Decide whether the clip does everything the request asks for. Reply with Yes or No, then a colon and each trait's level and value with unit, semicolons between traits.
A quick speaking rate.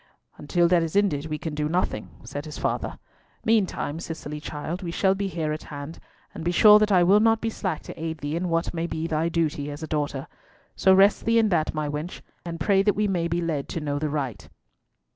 Yes: fast, 235 wpm